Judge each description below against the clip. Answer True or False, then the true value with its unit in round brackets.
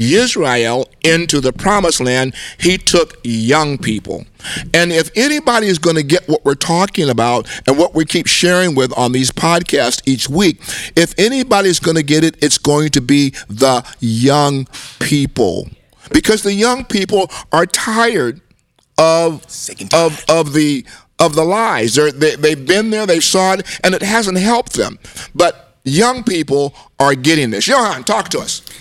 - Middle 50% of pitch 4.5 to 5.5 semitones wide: True (5.1 semitones)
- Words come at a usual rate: True (165 wpm)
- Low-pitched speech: False (160 Hz)